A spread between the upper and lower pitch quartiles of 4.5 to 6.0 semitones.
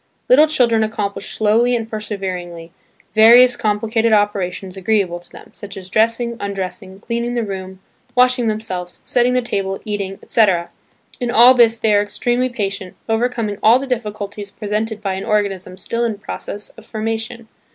No: average, 3.0 semitones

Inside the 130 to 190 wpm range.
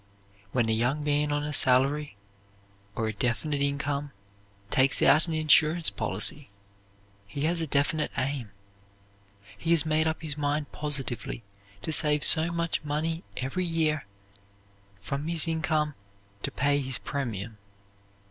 Yes: average, 140 wpm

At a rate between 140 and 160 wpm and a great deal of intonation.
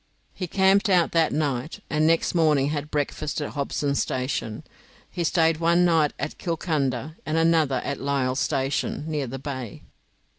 No: average, 155 wpm; average, 3.2 semitones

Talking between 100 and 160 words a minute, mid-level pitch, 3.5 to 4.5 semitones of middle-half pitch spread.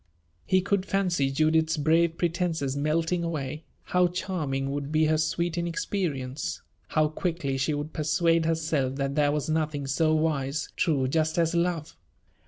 No: average, 150 wpm; medium, 155 Hz; average, 2.8 semitones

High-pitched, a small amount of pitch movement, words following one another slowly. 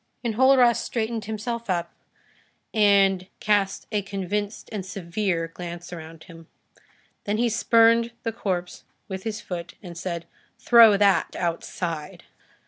No: high, 200 Hz; average, 4.1 semitones; slow, 125 wpm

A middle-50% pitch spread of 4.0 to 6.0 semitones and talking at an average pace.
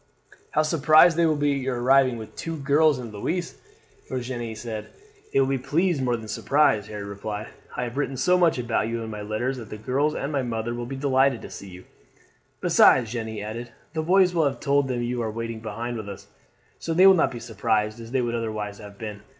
No: average, 4.4 semitones; fast, 230 wpm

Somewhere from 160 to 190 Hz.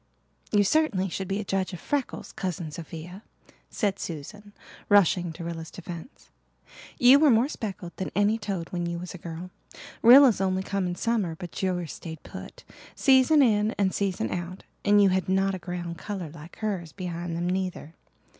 Yes: medium, 185 Hz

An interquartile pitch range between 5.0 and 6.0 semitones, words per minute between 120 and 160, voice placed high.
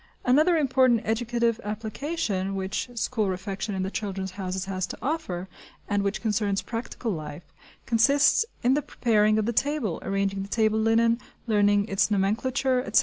No: average, 3.6 semitones; average, 155 wpm; high, 215 Hz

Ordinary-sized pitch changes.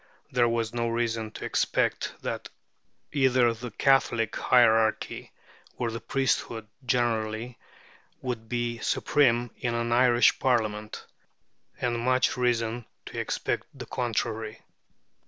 No: narrow, 1.6 semitones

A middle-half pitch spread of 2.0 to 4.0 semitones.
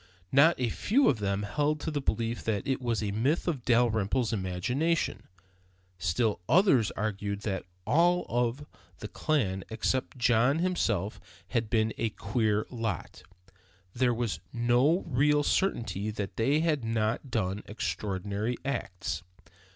No: average, 5.0 semitones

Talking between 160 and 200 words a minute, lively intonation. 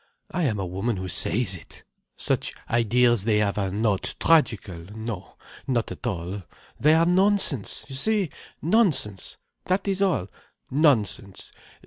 No: average, 140 wpm; wide, 8.6 semitones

